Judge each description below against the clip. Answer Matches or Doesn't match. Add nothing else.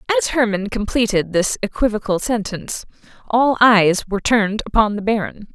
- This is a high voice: Matches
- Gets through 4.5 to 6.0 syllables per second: Matches